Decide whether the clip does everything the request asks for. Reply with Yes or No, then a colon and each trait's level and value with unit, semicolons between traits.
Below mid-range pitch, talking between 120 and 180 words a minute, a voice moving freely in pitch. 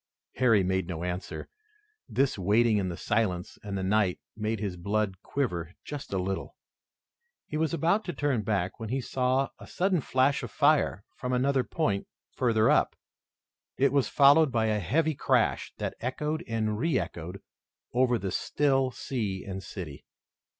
Yes: low, 115 Hz; average, 165 wpm; wide, 6.1 semitones